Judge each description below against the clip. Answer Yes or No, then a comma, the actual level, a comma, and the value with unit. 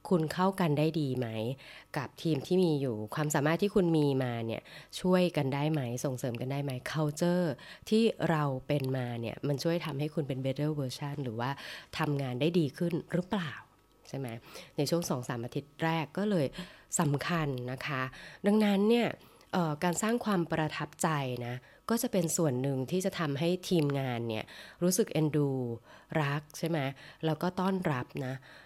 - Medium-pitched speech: Yes, medium, 150 Hz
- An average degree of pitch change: Yes, average, 4.6 semitones